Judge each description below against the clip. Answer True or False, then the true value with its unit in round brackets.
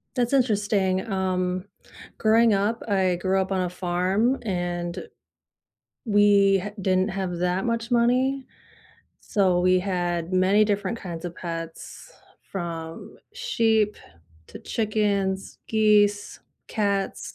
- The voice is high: True (195 Hz)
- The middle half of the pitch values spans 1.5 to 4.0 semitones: True (3.0 semitones)